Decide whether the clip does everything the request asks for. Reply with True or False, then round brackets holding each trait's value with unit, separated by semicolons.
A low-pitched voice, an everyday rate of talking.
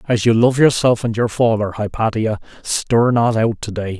True (115 Hz; 195 wpm)